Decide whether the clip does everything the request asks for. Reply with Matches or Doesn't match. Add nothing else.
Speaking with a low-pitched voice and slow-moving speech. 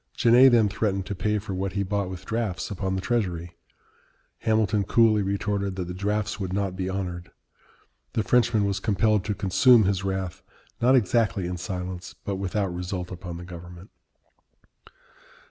Doesn't match